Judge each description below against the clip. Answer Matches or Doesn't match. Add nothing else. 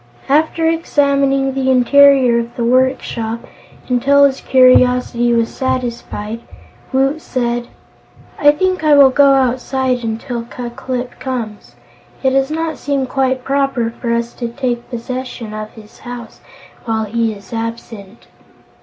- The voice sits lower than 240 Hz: Doesn't match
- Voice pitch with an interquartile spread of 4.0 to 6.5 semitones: Doesn't match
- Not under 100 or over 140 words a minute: Matches